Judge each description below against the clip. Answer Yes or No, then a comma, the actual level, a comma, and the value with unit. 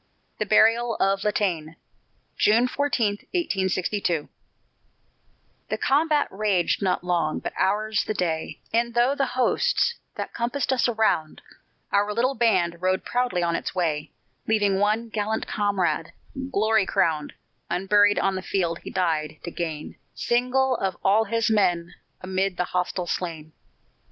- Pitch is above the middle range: Yes, high, 200 Hz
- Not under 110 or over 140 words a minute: Yes, slow, 135 wpm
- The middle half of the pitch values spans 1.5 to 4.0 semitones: No, average, 4.4 semitones